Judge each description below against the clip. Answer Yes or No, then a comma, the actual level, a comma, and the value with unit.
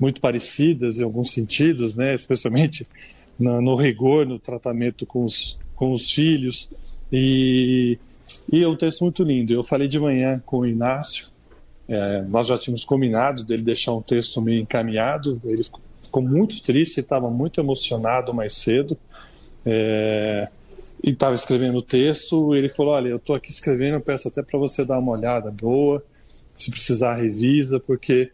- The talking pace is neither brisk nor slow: Yes, average, 165 wpm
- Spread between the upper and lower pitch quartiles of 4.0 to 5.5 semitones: No, average, 3.0 semitones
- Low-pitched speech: Yes, low, 125 Hz